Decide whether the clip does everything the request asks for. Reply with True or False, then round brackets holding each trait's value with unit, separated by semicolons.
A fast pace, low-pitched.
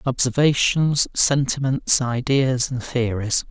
False (85 wpm; 130 Hz)